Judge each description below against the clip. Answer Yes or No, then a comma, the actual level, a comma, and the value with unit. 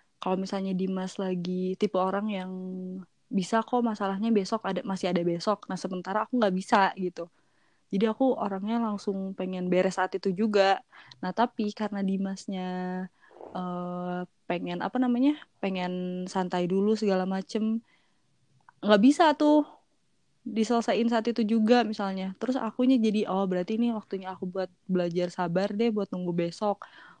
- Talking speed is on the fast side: Yes, fast, 145 wpm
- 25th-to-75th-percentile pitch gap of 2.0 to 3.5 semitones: Yes, average, 3.1 semitones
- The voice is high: Yes, high, 195 Hz